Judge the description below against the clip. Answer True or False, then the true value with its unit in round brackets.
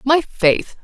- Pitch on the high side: True (250 Hz)